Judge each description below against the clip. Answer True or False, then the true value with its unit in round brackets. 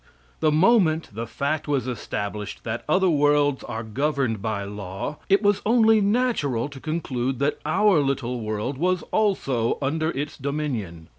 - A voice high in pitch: False (140 Hz)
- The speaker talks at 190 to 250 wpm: False (150 wpm)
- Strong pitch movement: True (5.7 semitones)